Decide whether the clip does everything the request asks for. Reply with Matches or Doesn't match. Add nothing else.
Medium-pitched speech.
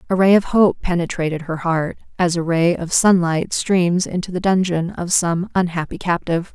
Matches